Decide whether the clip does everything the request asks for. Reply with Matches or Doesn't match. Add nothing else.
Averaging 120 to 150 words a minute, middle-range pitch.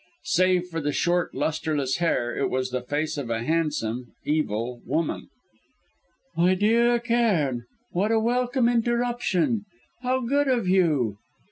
Matches